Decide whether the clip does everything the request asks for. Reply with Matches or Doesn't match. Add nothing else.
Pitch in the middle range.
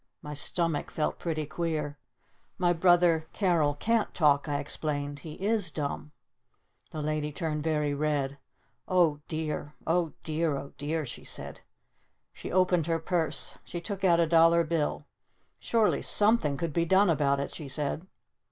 Matches